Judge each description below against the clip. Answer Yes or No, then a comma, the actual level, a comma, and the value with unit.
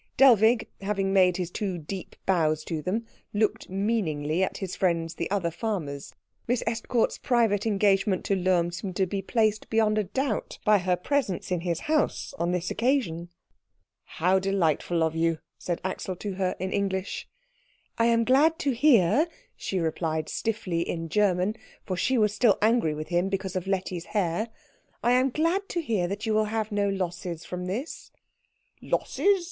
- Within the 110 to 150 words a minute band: No, average, 170 wpm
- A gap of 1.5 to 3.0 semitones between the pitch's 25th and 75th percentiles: No, average, 4.1 semitones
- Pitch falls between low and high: No, high, 195 Hz